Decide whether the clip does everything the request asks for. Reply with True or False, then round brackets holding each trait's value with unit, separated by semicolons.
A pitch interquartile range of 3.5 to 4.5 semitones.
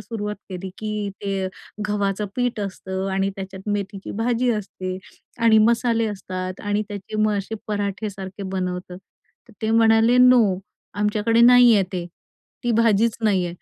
False (2.8 semitones)